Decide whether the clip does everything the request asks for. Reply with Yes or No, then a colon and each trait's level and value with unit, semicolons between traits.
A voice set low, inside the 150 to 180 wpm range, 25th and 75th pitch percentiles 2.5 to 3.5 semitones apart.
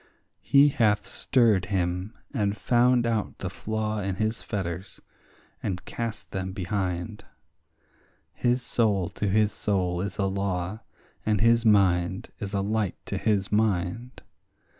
No: low, 105 Hz; slow, 135 wpm; average, 2.9 semitones